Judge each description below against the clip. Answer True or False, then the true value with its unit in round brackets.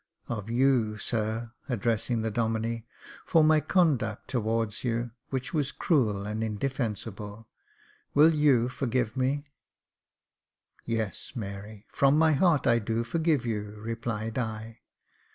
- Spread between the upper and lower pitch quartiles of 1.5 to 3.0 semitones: False (3.5 semitones)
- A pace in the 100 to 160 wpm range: True (135 wpm)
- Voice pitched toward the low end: True (115 Hz)